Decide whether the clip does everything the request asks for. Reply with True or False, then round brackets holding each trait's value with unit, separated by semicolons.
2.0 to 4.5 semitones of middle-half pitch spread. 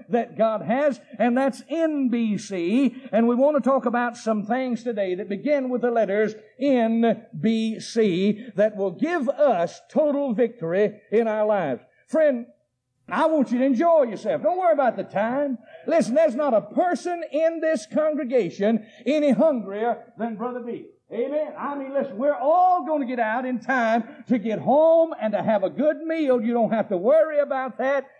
False (5.1 semitones)